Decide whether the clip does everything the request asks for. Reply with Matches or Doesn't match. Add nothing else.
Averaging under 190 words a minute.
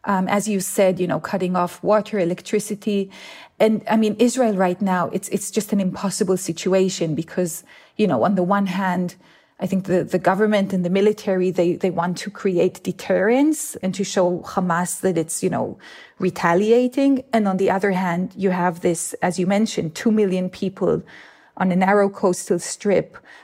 Matches